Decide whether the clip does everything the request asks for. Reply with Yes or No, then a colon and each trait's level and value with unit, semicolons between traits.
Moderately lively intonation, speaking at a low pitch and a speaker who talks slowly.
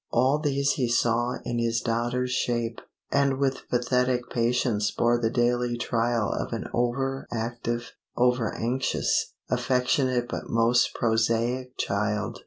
No: narrow, 1.4 semitones; low, 120 Hz; slow, 130 wpm